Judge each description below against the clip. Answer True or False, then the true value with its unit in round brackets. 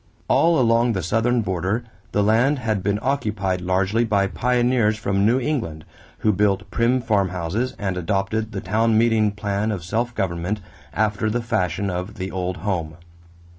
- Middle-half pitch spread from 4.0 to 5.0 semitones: False (3.5 semitones)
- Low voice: True (105 Hz)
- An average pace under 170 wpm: True (160 wpm)